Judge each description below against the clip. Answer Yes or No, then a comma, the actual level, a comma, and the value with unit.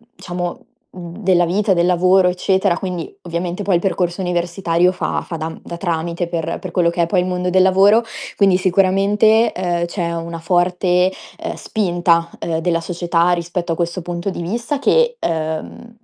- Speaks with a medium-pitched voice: Yes, medium, 180 Hz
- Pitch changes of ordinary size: No, narrow, 1.8 semitones